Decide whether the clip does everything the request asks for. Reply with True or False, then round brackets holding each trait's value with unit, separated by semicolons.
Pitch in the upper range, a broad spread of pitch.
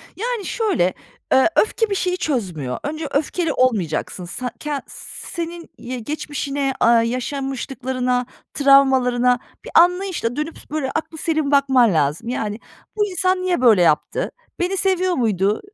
True (275 Hz; 6.1 semitones)